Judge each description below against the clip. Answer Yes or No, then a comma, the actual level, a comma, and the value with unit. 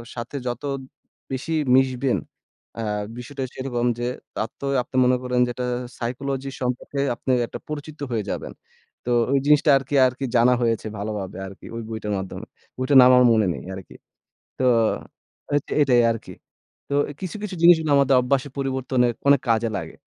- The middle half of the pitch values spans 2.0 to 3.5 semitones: Yes, average, 2.7 semitones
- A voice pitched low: Yes, low, 125 Hz